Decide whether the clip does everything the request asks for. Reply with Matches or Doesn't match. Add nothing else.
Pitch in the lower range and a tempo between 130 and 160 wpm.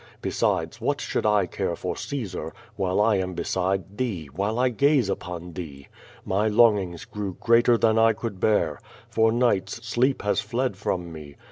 Doesn't match